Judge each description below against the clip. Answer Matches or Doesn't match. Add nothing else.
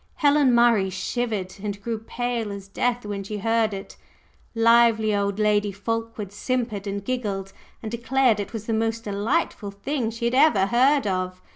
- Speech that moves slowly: Doesn't match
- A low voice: Doesn't match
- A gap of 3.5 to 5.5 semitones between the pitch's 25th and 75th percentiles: Doesn't match